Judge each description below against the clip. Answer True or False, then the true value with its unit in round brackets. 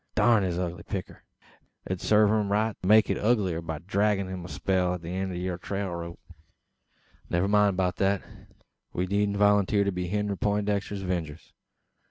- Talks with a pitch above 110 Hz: False (95 Hz)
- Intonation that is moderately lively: False (2.3 semitones)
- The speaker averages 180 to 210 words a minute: True (185 wpm)